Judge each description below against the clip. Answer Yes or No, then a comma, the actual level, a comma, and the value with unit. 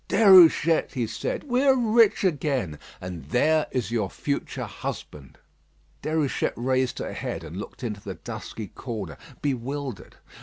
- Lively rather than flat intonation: Yes, wide, 7.0 semitones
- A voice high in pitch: No, low, 130 Hz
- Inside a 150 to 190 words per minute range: No, average, 140 wpm